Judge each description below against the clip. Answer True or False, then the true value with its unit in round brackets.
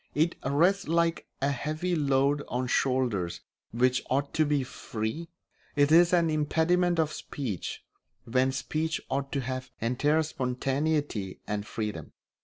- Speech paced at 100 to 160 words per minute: True (135 wpm)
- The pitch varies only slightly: False (3.8 semitones)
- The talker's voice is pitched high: False (140 Hz)